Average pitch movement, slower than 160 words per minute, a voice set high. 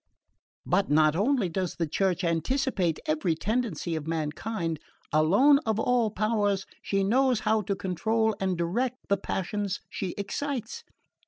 Yes: average, 4.9 semitones; average, 140 wpm; high, 200 Hz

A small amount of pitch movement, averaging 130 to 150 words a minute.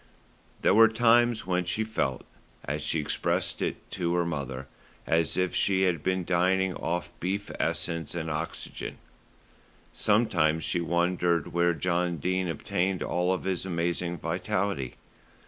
Yes: narrow, 2.2 semitones; slow, 135 wpm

